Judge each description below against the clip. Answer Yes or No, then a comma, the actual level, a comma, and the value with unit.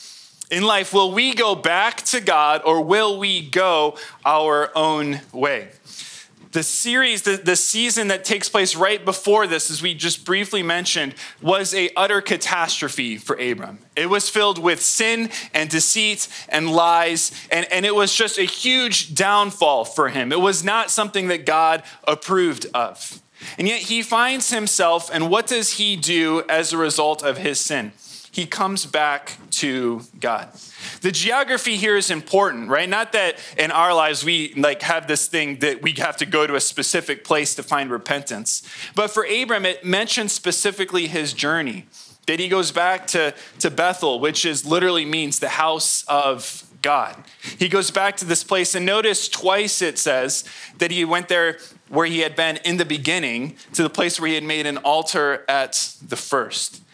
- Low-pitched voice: No, medium, 175 Hz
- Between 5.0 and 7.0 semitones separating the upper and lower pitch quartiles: No, average, 4.2 semitones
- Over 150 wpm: Yes, average, 180 wpm